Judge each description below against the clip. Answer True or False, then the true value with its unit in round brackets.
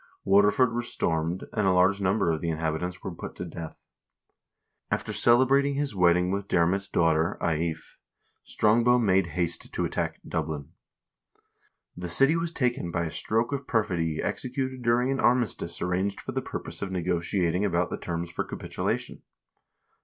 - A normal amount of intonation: False (5.9 semitones)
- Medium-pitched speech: False (95 Hz)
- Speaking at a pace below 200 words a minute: True (160 wpm)